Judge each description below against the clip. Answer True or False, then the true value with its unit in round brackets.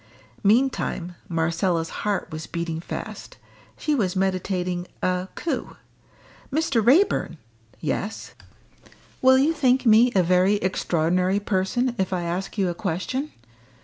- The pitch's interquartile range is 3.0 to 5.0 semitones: False (5.5 semitones)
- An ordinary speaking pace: False (120 wpm)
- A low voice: False (190 Hz)